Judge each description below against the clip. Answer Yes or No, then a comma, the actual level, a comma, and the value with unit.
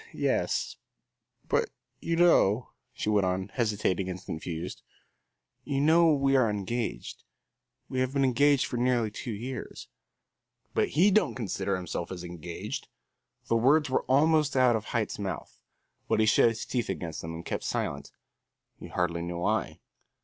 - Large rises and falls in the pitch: Yes, wide, 6.3 semitones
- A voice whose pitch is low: Yes, low, 115 Hz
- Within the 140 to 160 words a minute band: Yes, average, 155 wpm